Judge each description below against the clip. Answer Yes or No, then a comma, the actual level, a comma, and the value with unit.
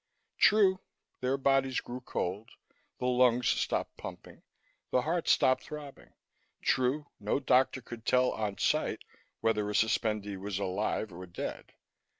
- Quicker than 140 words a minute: No, slow, 135 wpm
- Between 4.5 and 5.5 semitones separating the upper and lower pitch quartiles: No, average, 4.1 semitones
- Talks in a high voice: No, low, 125 Hz